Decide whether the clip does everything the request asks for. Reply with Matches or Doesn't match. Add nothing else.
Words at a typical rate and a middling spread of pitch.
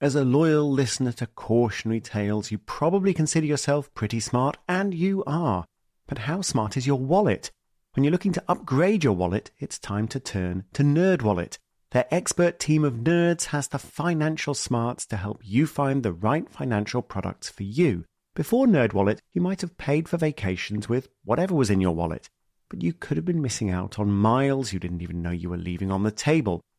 Doesn't match